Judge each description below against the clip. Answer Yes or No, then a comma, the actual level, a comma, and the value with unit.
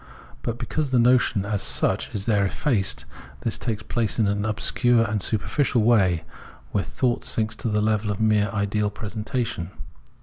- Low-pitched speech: Yes, low, 110 Hz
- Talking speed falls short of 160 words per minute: No, average, 165 wpm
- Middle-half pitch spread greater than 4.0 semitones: No, narrow, 2.6 semitones